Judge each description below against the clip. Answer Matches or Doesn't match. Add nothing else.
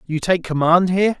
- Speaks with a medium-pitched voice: Matches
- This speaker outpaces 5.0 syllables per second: Matches